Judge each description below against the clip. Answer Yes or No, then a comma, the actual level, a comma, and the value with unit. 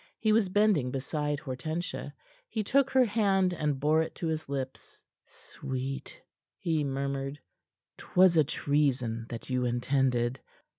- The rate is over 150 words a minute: No, slow, 135 wpm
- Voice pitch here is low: No, medium, 145 Hz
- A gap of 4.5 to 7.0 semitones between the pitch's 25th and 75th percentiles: Yes, average, 5.2 semitones